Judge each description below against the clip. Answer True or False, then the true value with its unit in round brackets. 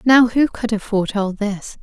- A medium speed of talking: True (195 wpm)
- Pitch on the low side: False (220 Hz)